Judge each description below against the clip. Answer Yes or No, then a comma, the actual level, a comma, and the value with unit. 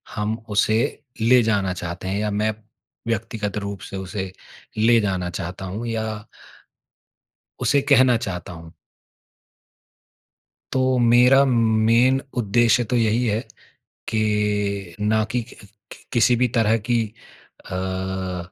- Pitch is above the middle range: No, low, 110 Hz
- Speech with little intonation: No, average, 3.3 semitones